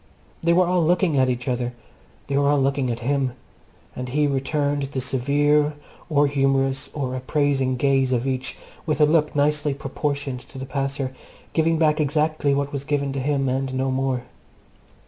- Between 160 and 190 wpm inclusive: Yes, average, 175 wpm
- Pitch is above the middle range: No, medium, 140 Hz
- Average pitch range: No, narrow, 2.0 semitones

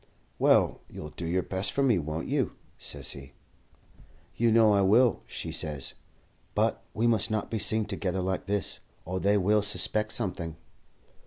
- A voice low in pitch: Yes, low, 100 Hz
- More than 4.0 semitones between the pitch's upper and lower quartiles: No, average, 3.2 semitones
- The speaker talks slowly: No, average, 165 wpm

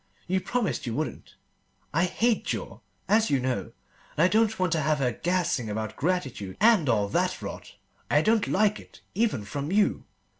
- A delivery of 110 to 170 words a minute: No, average, 180 wpm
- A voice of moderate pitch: Yes, medium, 170 Hz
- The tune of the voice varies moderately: No, wide, 8.4 semitones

